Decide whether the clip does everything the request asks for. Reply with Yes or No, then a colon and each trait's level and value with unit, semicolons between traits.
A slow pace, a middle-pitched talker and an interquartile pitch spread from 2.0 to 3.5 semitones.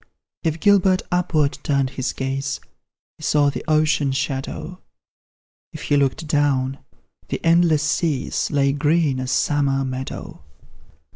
Yes: slow, 125 wpm; medium, 145 Hz; average, 2.7 semitones